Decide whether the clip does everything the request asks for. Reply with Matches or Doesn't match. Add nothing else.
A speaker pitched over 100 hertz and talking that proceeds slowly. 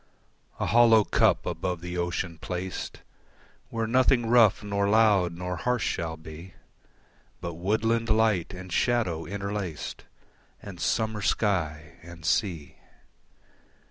Doesn't match